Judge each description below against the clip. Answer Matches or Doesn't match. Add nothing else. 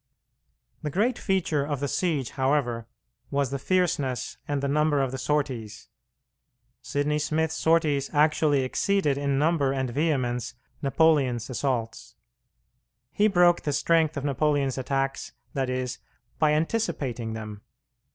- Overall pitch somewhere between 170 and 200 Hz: Doesn't match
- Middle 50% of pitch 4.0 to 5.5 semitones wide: Doesn't match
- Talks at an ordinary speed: Doesn't match